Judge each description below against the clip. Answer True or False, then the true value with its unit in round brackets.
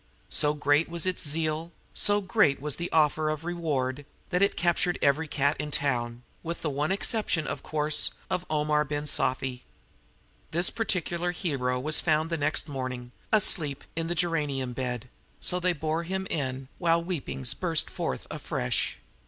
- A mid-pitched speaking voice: True (155 Hz)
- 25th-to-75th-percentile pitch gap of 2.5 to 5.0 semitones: True (3.6 semitones)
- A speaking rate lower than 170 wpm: True (160 wpm)